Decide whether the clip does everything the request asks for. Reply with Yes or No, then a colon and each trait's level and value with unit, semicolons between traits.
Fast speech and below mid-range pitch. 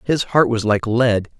Yes: fast, 215 wpm; low, 115 Hz